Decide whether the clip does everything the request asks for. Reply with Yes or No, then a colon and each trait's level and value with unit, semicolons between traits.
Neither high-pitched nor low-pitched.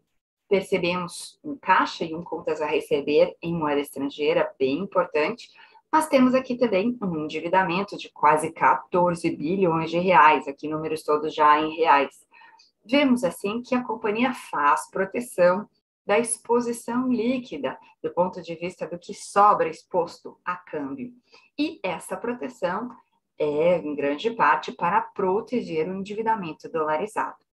No: high, 195 Hz